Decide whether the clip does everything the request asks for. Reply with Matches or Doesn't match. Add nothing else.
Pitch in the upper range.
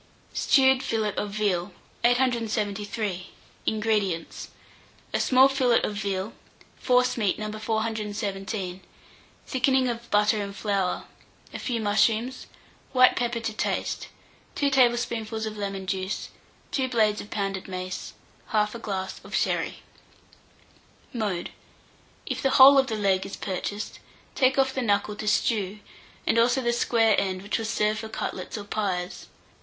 Matches